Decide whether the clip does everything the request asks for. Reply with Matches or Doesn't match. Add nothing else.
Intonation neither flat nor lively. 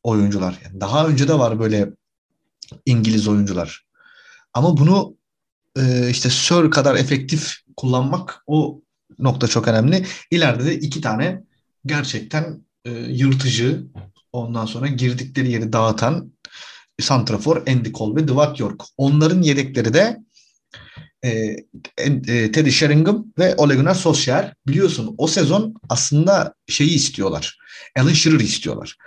Matches